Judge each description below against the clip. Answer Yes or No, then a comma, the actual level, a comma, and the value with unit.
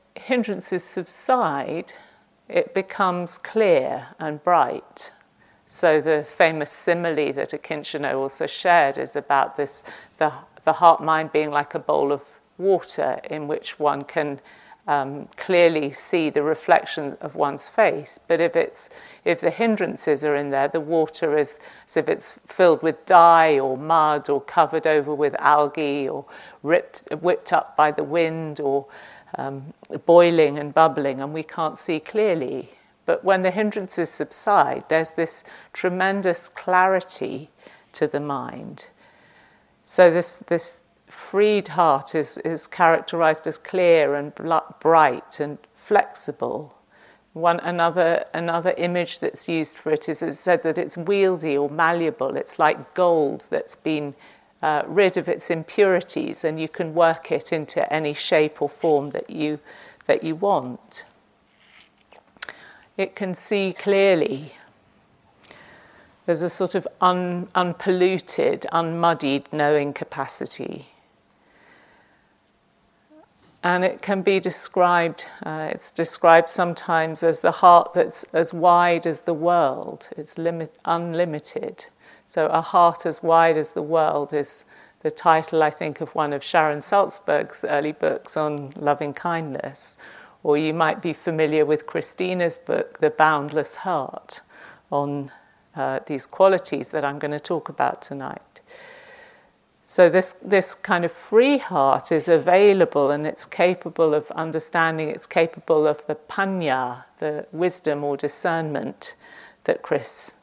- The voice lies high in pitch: No, medium, 165 Hz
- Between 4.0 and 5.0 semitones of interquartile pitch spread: No, average, 3.0 semitones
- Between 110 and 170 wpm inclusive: Yes, average, 140 wpm